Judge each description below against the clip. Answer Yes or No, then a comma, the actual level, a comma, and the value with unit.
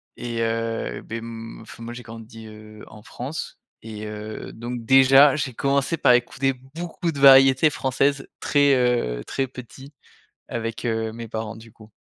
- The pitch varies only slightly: No, average, 3.2 semitones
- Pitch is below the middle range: Yes, low, 120 Hz